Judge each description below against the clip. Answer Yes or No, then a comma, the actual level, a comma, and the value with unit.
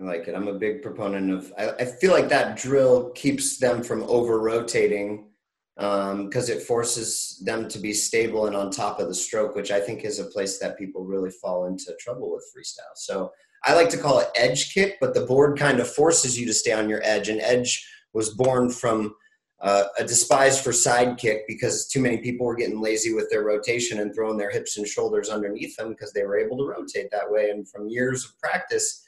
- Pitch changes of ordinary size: Yes, average, 4.6 semitones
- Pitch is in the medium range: No, low, 115 Hz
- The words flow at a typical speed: No, fast, 225 wpm